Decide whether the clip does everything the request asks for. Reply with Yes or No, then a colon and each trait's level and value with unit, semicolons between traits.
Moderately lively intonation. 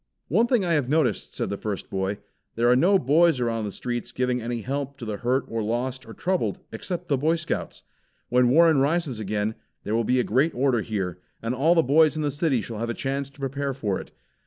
Yes: average, 4.8 semitones